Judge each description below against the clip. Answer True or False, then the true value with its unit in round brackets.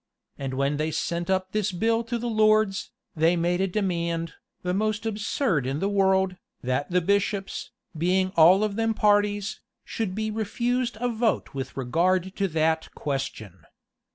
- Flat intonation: False (4.4 semitones)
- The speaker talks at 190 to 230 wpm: False (160 wpm)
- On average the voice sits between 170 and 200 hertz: True (190 Hz)